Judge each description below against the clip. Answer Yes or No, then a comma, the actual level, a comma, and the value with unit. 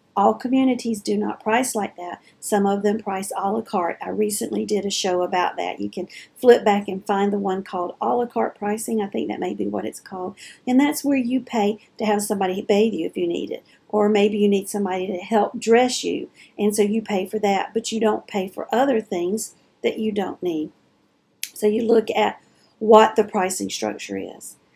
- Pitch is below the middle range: No, high, 210 Hz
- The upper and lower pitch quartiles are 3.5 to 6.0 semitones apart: No, average, 2.8 semitones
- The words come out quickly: Yes, fast, 220 wpm